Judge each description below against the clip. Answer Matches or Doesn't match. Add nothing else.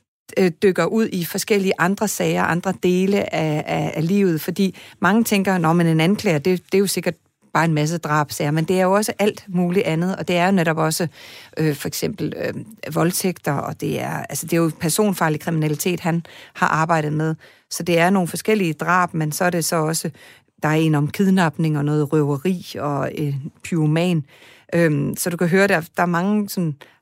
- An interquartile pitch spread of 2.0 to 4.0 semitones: Matches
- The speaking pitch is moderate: Matches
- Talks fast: Doesn't match